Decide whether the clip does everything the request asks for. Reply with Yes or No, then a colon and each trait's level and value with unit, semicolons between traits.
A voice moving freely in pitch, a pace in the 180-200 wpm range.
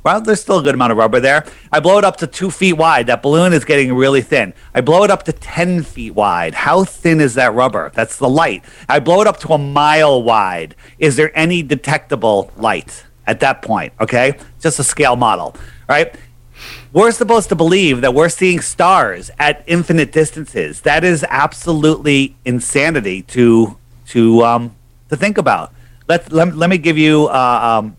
Yes: wide, 5.7 semitones; average, 195 wpm